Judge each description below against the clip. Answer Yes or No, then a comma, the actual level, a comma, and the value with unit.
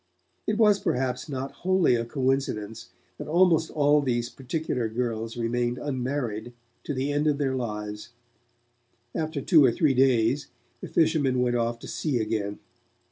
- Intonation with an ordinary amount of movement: Yes, average, 3.9 semitones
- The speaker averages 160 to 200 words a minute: No, average, 150 wpm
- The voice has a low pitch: Yes, low, 130 Hz